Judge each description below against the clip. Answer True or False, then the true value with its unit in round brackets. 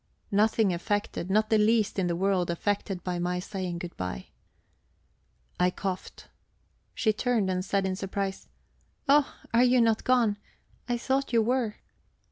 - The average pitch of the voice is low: False (200 Hz)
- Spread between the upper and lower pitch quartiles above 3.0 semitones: True (3.7 semitones)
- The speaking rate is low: False (150 wpm)